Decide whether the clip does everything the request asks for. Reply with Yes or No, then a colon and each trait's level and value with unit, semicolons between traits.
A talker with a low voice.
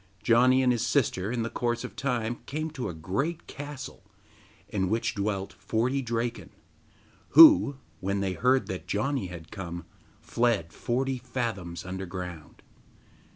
Yes: low, 115 Hz